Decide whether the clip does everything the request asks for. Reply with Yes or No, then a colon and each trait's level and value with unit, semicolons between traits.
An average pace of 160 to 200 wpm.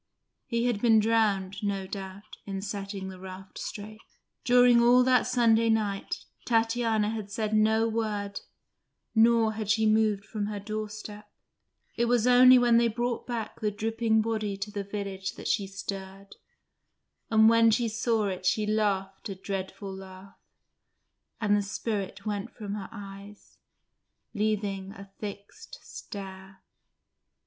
No: average, 140 wpm